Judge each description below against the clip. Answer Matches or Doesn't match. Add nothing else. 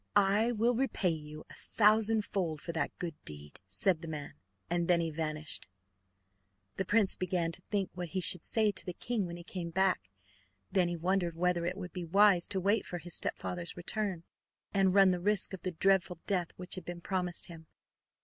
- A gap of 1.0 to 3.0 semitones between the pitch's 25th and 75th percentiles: Matches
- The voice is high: Doesn't match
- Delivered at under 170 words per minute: Doesn't match